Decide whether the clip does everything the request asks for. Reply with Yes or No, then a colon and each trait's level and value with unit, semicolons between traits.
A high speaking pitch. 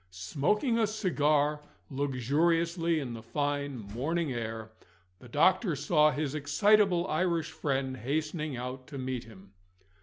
No: medium, 145 Hz